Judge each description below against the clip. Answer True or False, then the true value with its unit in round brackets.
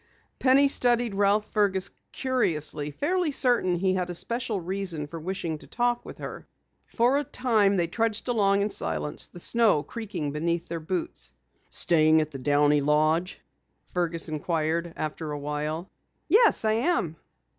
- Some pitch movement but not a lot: False (6.6 semitones)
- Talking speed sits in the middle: True (150 wpm)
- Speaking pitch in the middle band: True (180 Hz)